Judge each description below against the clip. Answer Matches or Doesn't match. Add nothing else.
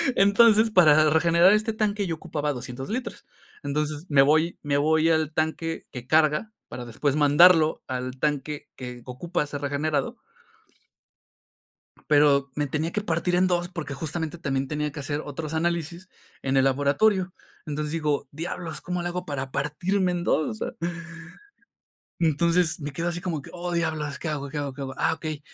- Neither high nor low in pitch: Matches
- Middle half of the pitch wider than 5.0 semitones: Doesn't match